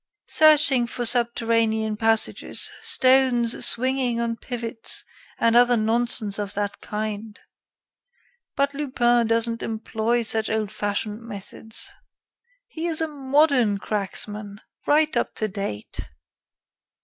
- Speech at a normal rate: No, slow, 110 wpm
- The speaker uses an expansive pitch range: No, average, 2.8 semitones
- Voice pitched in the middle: No, high, 230 Hz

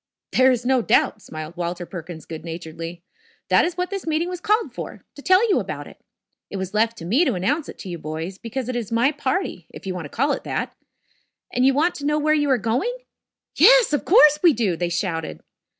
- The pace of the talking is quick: Yes, fast, 230 wpm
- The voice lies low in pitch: No, high, 240 Hz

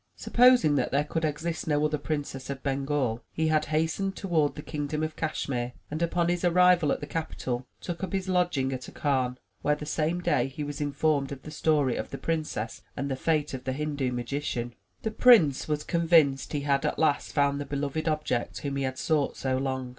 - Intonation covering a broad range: No, average, 2.8 semitones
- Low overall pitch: No, medium, 150 Hz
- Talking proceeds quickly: Yes, fast, 210 wpm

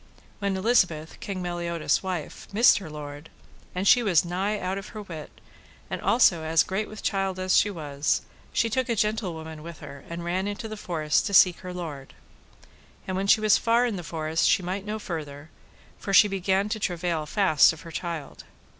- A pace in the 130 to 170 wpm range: No, average, 195 wpm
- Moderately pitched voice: Yes, medium, 180 Hz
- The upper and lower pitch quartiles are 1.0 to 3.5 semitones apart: No, average, 4.0 semitones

